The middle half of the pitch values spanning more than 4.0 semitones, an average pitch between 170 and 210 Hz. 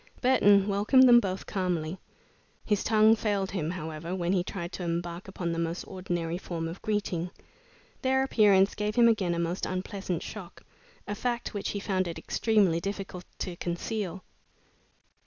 No: average, 3.3 semitones; high, 190 Hz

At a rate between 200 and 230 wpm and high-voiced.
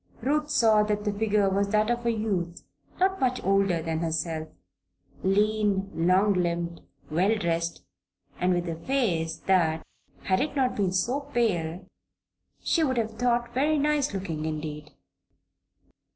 No: average, 145 wpm; high, 200 Hz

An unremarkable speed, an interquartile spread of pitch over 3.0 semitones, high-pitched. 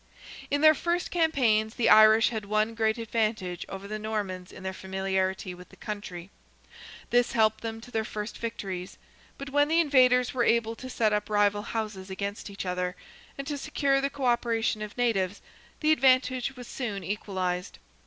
Yes: average, 175 wpm; average, 4.1 semitones; high, 220 Hz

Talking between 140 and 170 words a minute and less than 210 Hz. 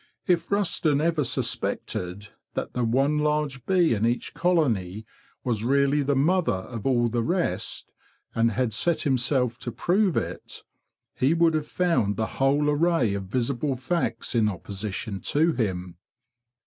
Yes: average, 150 wpm; low, 135 Hz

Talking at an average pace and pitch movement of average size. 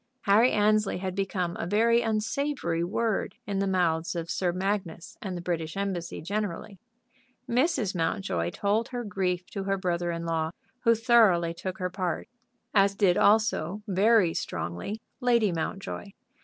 Yes: average, 150 wpm; average, 3.7 semitones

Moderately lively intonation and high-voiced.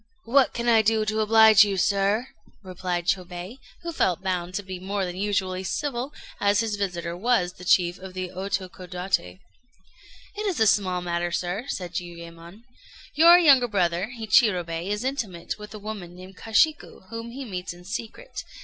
Yes: average, 3.8 semitones; high, 195 Hz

